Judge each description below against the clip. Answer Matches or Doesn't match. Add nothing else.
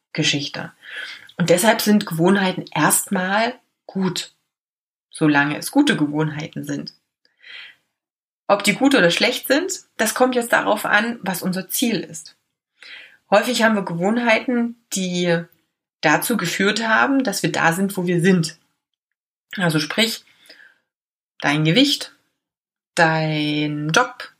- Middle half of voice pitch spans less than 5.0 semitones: Doesn't match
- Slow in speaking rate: Matches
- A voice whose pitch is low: Doesn't match